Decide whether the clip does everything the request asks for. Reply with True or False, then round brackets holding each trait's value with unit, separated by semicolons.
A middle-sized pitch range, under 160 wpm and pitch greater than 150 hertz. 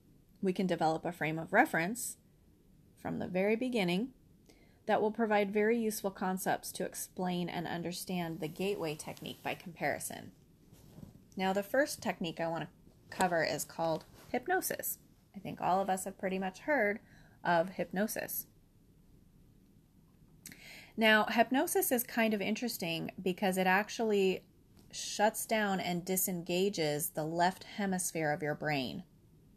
True (3.9 semitones; 135 wpm; 190 Hz)